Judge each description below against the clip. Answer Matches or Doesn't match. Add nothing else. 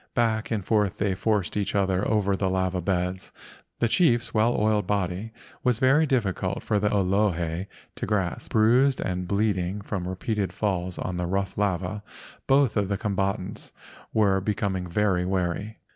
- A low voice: Matches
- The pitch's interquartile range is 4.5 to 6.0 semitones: Doesn't match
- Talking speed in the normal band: Matches